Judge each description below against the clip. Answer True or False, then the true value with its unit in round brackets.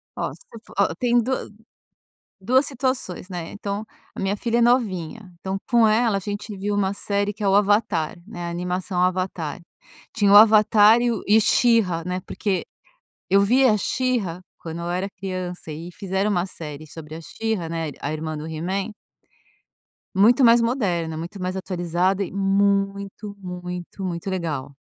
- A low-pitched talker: False (195 Hz)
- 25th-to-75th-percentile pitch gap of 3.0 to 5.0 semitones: True (3.3 semitones)